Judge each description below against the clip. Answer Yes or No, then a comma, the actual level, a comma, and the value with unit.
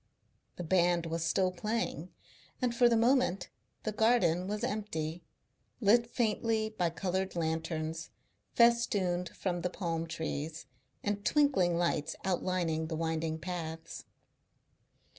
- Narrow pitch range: No, average, 4.7 semitones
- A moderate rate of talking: No, slow, 120 wpm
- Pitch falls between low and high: Yes, medium, 180 Hz